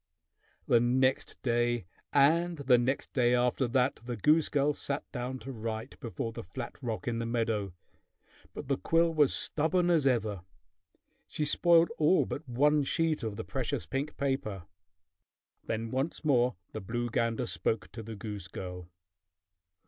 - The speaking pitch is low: Yes, low, 125 Hz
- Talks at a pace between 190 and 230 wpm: No, average, 155 wpm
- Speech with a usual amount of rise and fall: Yes, average, 4.1 semitones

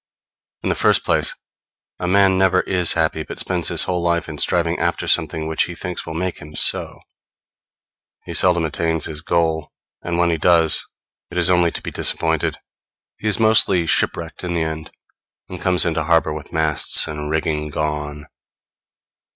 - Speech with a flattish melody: Yes, narrow, 2.2 semitones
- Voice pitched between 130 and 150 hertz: No, very low, 80 Hz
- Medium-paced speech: Yes, average, 175 wpm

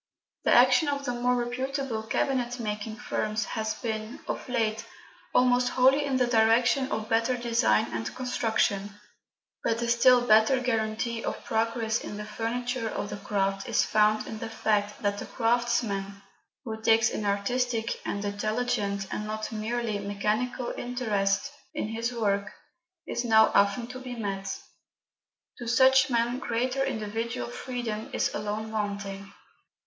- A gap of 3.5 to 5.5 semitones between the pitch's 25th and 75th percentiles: No, narrow, 2.6 semitones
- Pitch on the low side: No, high, 225 Hz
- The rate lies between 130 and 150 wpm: Yes, average, 145 wpm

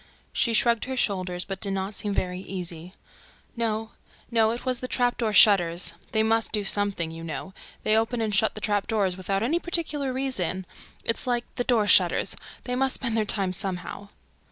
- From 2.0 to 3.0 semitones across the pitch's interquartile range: No, average, 3.8 semitones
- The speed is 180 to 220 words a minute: Yes, average, 185 wpm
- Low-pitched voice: No, high, 215 Hz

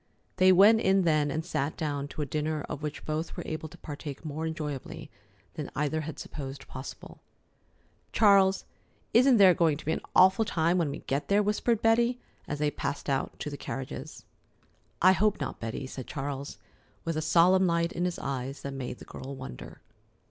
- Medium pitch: Yes, medium, 155 Hz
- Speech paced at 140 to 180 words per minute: No, average, 190 wpm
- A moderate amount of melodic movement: Yes, average, 4.6 semitones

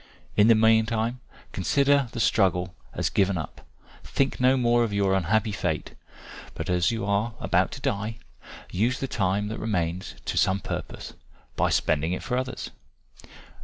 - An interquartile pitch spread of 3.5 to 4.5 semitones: Yes, average, 3.8 semitones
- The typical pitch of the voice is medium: No, low, 105 Hz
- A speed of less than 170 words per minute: Yes, average, 160 wpm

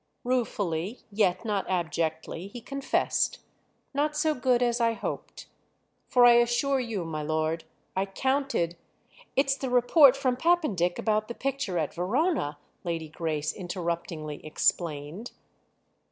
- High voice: Yes, high, 210 Hz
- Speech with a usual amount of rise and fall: No, wide, 7.4 semitones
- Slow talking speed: Yes, slow, 125 wpm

